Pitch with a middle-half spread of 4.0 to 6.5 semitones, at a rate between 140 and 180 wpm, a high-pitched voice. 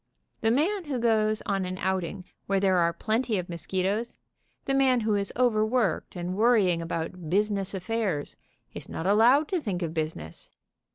Yes: average, 4.3 semitones; average, 165 wpm; high, 200 Hz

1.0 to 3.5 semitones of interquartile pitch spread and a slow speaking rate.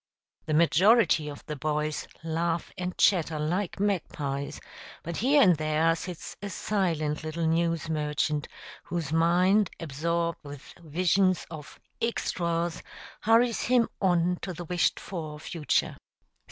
Yes: average, 3.0 semitones; slow, 125 wpm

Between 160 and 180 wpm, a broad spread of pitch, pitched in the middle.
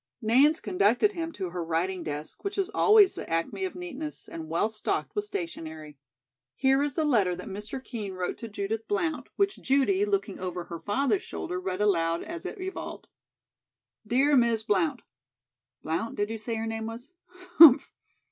No: average, 175 wpm; wide, 9.0 semitones; high, 225 Hz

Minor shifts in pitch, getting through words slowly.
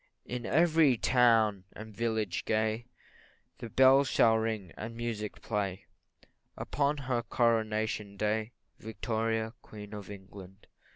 Yes: narrow, 2.1 semitones; slow, 115 wpm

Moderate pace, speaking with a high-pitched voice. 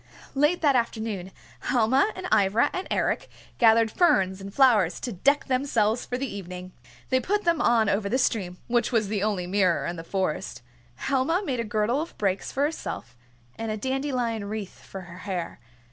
Yes: average, 180 wpm; high, 220 Hz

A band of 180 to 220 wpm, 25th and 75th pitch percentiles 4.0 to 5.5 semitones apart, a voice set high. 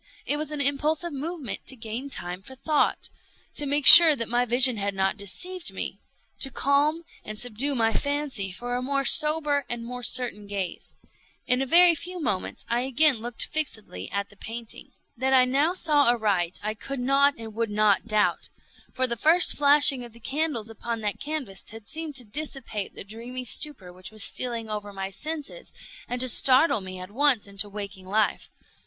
Yes: average, 185 wpm; average, 5.2 semitones; high, 245 Hz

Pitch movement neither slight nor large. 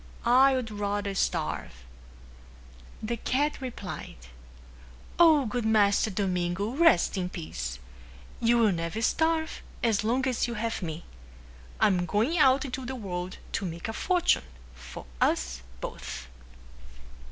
No: wide, 6.4 semitones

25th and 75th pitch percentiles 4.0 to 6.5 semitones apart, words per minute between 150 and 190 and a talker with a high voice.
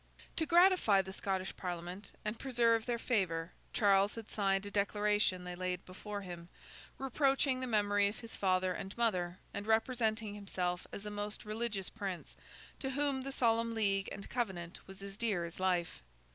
No: average, 3.6 semitones; average, 170 wpm; high, 205 Hz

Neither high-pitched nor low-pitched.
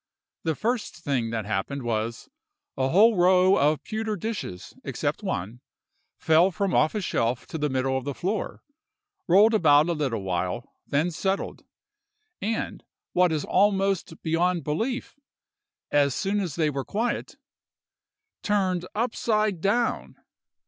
Yes: medium, 170 Hz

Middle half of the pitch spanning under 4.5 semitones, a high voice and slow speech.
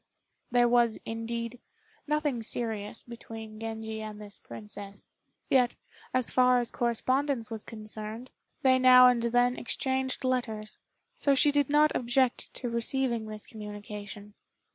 Yes: average, 2.8 semitones; high, 235 Hz; slow, 130 wpm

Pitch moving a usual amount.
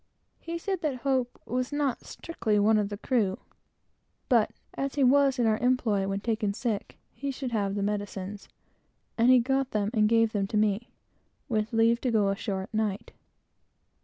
Yes: average, 3.8 semitones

